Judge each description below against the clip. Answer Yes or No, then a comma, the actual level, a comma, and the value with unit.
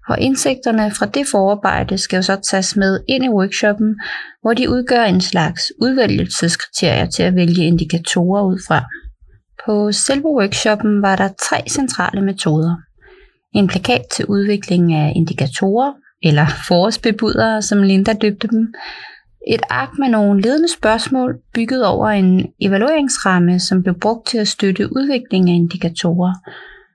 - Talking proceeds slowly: Yes, slow, 140 wpm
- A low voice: No, high, 205 Hz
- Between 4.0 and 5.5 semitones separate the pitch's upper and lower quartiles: Yes, average, 4.5 semitones